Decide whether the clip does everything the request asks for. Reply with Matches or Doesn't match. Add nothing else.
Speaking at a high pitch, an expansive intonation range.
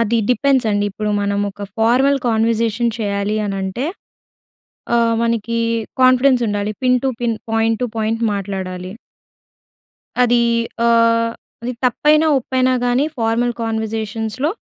Doesn't match